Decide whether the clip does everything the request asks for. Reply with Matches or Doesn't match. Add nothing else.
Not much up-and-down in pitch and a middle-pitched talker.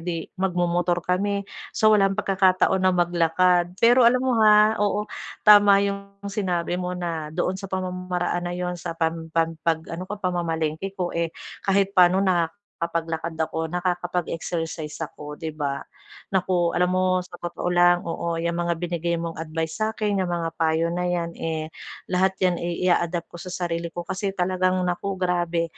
Matches